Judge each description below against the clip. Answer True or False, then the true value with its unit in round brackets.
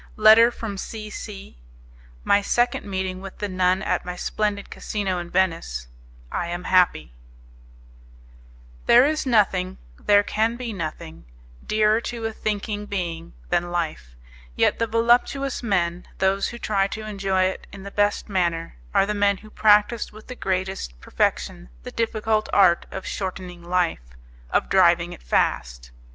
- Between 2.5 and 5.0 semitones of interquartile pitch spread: True (3.4 semitones)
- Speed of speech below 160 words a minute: True (150 wpm)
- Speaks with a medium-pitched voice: False (195 Hz)